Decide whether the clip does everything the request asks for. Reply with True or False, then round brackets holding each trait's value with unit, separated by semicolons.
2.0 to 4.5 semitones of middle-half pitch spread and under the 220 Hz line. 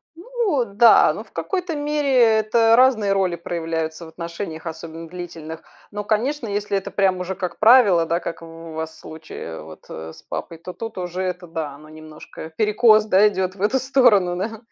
False (5.4 semitones; 190 Hz)